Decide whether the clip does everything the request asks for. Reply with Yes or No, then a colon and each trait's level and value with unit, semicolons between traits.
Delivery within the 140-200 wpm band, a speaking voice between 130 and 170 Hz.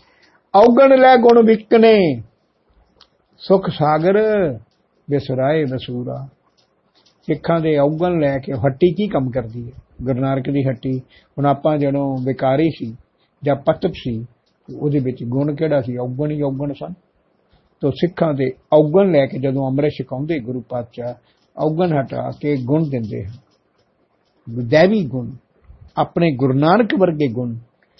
No: average, 130 wpm; medium, 140 Hz